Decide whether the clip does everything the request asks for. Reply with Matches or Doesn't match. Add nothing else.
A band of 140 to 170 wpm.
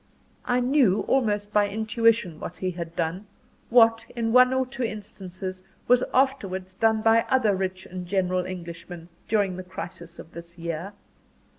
Matches